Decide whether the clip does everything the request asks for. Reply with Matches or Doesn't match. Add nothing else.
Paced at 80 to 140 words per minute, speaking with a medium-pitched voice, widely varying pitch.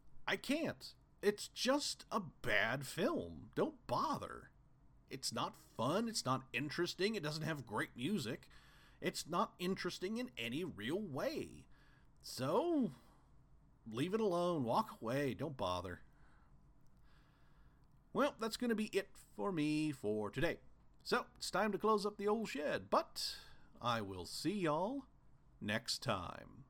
Matches